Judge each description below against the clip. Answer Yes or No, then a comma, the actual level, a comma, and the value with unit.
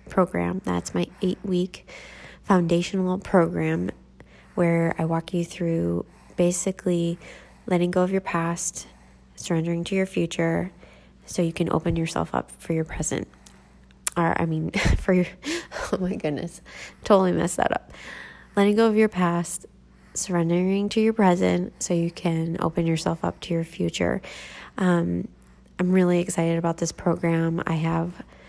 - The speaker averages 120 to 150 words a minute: Yes, average, 145 wpm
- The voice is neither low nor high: Yes, medium, 170 Hz